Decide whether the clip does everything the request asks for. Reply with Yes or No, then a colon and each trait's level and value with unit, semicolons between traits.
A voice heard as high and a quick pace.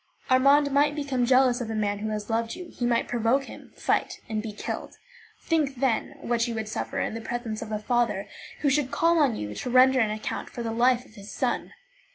Yes: high, 240 Hz; fast, 220 wpm